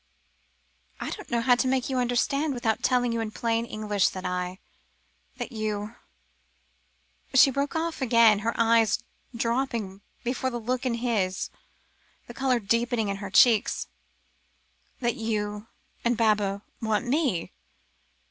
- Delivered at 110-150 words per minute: Yes, average, 140 wpm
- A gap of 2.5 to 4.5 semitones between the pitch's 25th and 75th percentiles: Yes, average, 2.9 semitones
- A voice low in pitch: No, high, 230 Hz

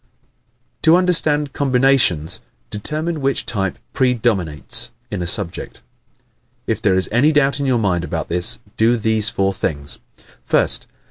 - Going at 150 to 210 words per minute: No, average, 140 wpm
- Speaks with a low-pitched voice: Yes, low, 115 Hz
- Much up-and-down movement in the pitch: Yes, wide, 7.0 semitones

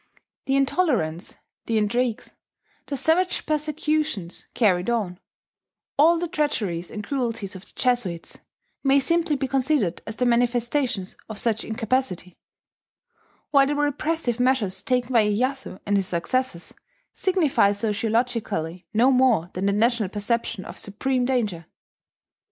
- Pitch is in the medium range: No, high, 240 Hz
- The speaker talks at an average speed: No, slow, 130 wpm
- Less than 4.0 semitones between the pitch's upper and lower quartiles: No, average, 5.1 semitones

